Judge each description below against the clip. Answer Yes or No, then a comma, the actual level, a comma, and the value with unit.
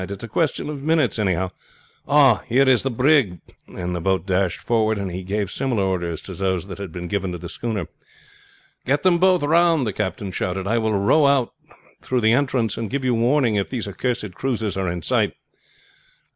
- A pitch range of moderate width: No, wide, 5.8 semitones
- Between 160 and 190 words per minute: No, average, 200 wpm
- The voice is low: Yes, low, 110 Hz